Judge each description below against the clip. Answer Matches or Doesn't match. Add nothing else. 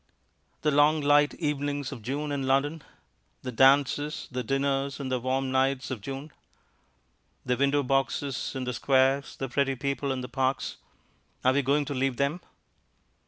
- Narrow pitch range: Matches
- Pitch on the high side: Doesn't match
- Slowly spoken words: Doesn't match